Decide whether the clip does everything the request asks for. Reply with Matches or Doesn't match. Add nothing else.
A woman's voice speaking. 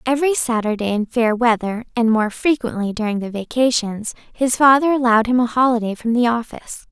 Matches